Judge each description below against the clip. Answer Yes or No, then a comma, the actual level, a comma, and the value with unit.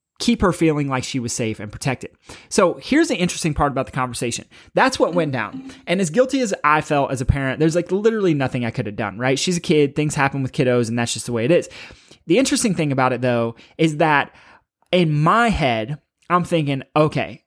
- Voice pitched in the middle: Yes, medium, 150 Hz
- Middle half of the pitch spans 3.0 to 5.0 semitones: No, wide, 5.5 semitones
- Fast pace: Yes, fast, 230 wpm